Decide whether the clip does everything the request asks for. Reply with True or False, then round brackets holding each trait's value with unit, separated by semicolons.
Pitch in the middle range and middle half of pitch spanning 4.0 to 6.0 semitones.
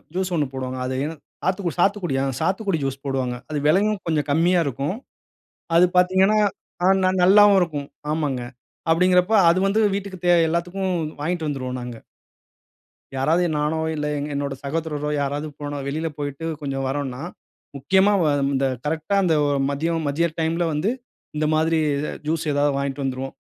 True (155 Hz; 4.3 semitones)